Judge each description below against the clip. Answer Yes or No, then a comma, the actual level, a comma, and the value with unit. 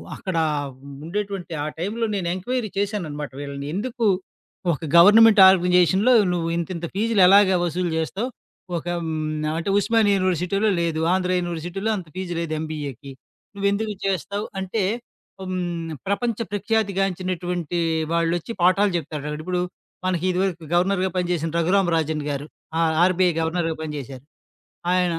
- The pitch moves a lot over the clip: No, average, 3.2 semitones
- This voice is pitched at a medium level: Yes, medium, 180 Hz